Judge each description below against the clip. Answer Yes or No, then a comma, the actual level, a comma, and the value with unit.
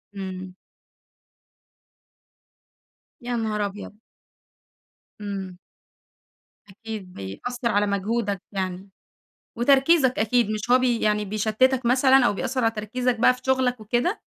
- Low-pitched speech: No, high, 225 Hz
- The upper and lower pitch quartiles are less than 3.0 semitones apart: No, average, 3.7 semitones